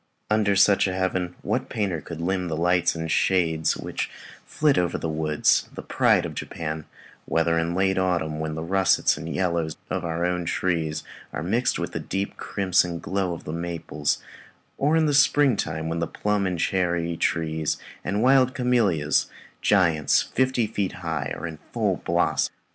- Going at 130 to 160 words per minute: No, average, 170 wpm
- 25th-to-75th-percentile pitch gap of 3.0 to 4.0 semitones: Yes, average, 3.3 semitones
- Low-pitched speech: Yes, very low, 90 Hz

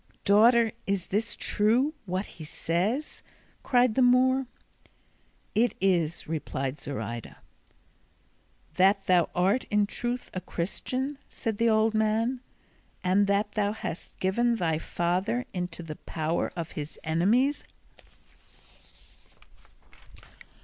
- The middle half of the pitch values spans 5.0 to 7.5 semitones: Yes, wide, 5.4 semitones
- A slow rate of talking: Yes, slow, 110 wpm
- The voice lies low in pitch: No, high, 200 Hz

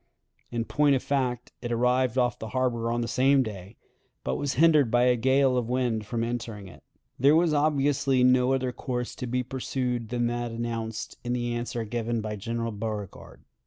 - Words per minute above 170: Yes, average, 190 wpm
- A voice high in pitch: No, low, 120 Hz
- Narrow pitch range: Yes, narrow, 2.0 semitones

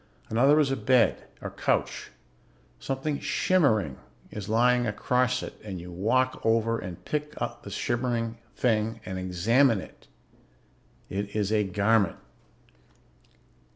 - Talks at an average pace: No, slow, 125 wpm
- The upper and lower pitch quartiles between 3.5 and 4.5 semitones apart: Yes, average, 3.9 semitones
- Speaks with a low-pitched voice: Yes, low, 115 Hz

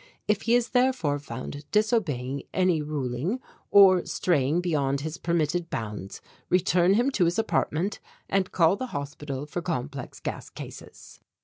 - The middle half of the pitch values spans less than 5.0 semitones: No, wide, 5.4 semitones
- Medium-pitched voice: Yes, medium, 170 Hz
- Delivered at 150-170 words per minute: No, average, 140 wpm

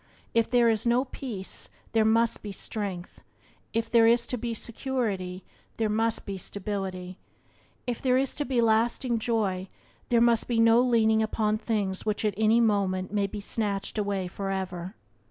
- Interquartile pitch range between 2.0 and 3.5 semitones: Yes, average, 2.9 semitones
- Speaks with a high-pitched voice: Yes, high, 220 Hz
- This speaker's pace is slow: No, average, 165 wpm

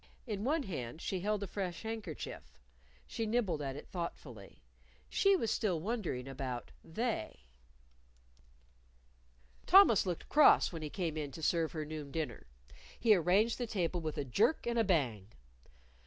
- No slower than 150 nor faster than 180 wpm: Yes, average, 155 wpm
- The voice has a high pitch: No, medium, 175 Hz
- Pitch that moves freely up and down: Yes, wide, 6.7 semitones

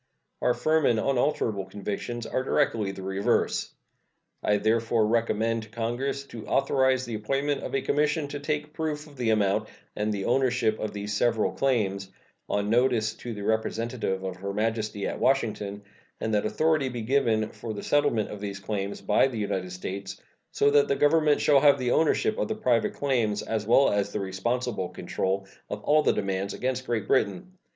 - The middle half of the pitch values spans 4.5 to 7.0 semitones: Yes, average, 4.8 semitones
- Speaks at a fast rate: No, average, 180 wpm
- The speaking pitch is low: Yes, low, 115 Hz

